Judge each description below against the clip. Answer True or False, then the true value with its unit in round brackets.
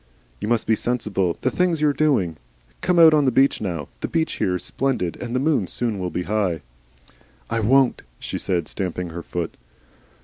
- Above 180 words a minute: True (200 wpm)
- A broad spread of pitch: True (7.2 semitones)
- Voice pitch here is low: True (110 Hz)